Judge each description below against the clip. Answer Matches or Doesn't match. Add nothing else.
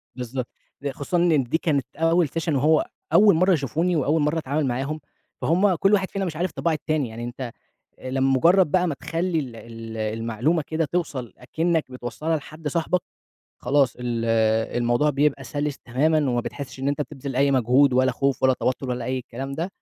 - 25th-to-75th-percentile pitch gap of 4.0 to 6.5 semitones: Matches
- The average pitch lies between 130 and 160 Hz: Matches